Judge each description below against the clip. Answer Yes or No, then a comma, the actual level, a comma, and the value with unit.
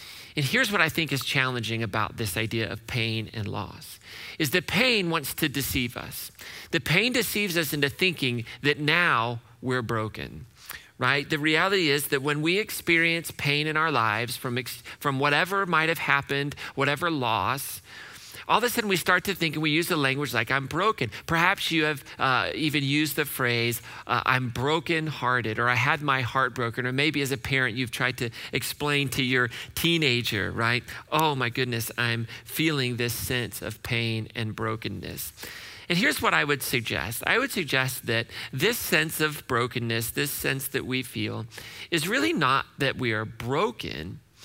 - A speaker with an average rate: Yes, average, 180 wpm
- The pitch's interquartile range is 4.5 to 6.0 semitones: Yes, average, 4.9 semitones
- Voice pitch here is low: Yes, low, 130 Hz